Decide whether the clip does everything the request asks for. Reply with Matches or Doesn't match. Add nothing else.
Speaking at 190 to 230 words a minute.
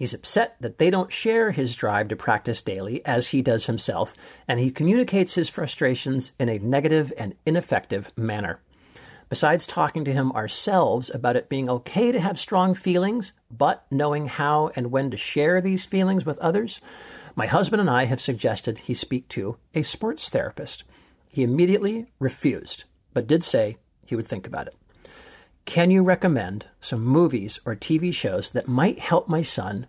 Doesn't match